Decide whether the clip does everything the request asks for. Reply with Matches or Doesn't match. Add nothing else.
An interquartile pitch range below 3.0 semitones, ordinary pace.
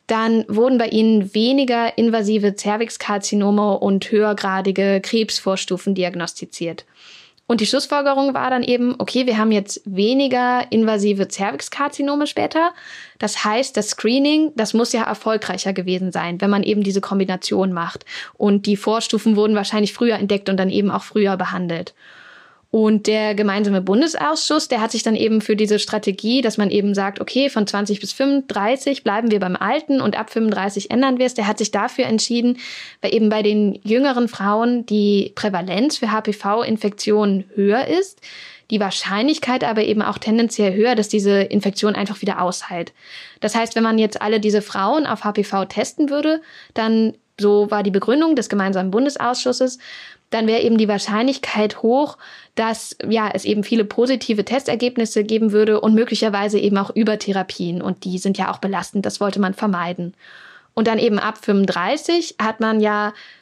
Matches